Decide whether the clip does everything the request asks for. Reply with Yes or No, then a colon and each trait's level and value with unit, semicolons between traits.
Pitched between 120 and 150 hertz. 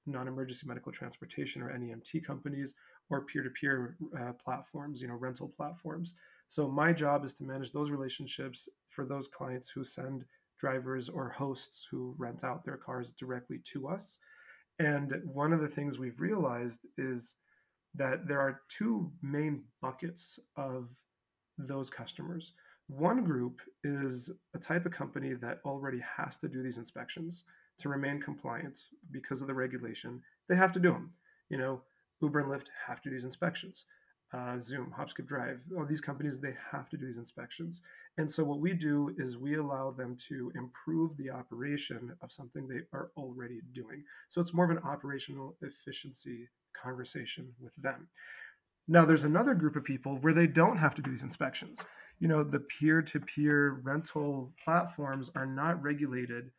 Yes: medium, 140 Hz